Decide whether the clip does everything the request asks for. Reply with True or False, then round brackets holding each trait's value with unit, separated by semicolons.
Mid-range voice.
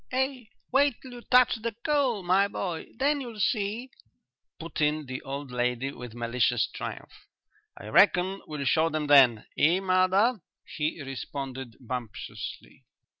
True (165 Hz)